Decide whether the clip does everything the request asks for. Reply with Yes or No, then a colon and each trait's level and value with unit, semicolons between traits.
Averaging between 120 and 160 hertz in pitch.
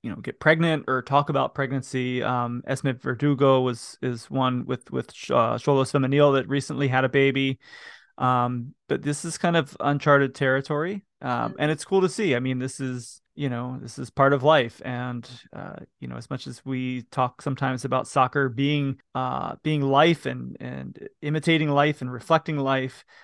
Yes: low, 135 Hz